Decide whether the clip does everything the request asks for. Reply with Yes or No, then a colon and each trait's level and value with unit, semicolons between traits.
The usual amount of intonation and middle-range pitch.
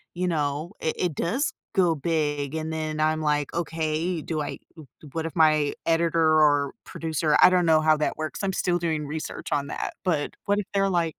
No: narrow, 1.9 semitones; medium, 160 Hz